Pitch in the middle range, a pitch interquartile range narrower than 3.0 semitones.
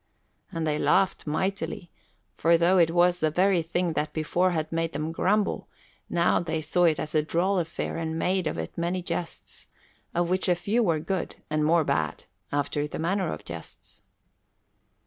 Yes: medium, 170 Hz; narrow, 2.4 semitones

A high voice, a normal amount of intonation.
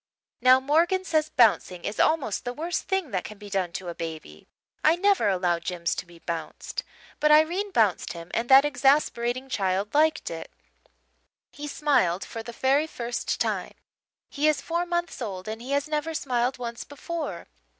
No: very high, 255 Hz; wide, 7.9 semitones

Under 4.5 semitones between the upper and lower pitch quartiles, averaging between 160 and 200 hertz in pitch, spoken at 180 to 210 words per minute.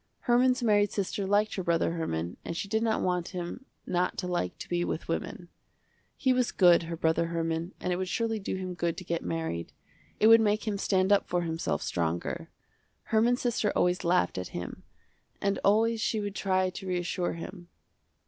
Yes: average, 3.8 semitones; medium, 185 Hz; average, 195 wpm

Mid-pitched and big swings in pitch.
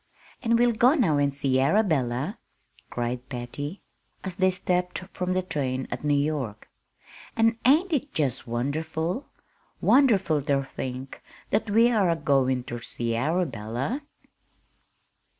Yes: medium, 155 Hz; wide, 7.7 semitones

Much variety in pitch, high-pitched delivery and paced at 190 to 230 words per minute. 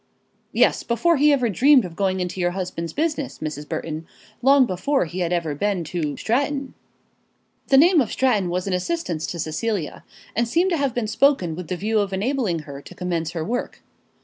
Yes: wide, 7.7 semitones; high, 195 Hz; average, 195 wpm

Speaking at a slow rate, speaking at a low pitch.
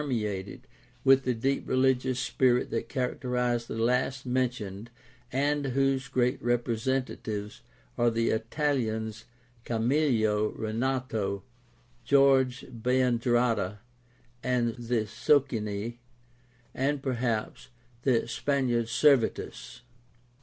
Yes: slow, 85 wpm; low, 125 Hz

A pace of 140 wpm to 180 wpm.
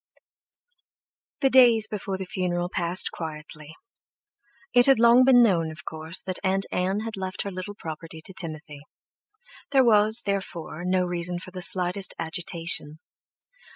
Yes: average, 145 wpm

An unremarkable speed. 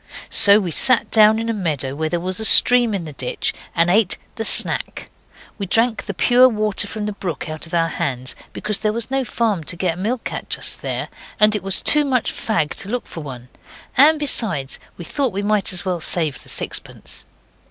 No: fast, 215 wpm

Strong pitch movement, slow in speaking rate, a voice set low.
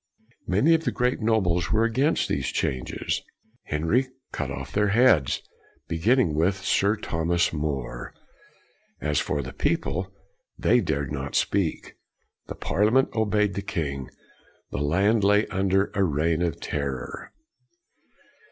Yes: wide, 6.0 semitones; slow, 130 wpm; very low, 90 Hz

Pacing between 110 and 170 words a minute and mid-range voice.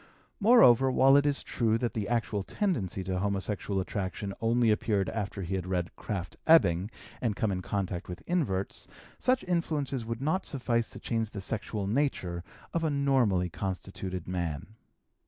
No: average, 160 wpm; low, 105 Hz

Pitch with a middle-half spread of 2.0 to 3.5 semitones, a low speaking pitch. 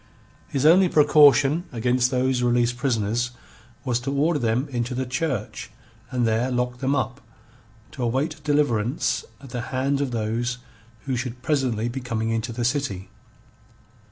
Yes: narrow, 2.6 semitones; low, 125 Hz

